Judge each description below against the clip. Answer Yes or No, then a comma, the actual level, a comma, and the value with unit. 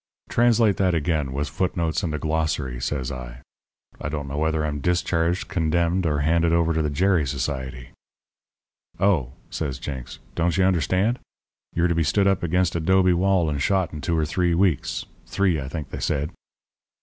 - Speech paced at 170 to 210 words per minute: Yes, average, 185 wpm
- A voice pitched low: Yes, very low, 80 Hz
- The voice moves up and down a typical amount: Yes, average, 3.7 semitones